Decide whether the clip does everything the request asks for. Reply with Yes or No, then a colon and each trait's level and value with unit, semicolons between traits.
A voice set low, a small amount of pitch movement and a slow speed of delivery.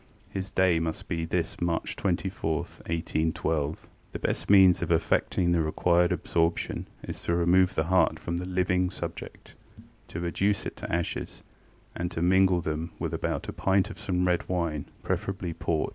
No: very low, 85 Hz; narrow, 2.0 semitones; average, 165 wpm